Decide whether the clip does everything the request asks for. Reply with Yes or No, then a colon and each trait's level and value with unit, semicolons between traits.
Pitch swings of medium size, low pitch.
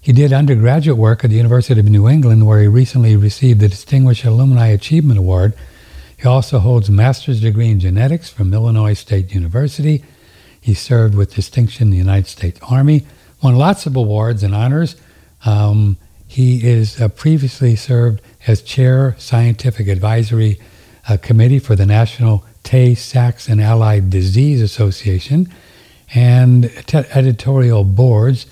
Yes: average, 3.5 semitones; low, 115 Hz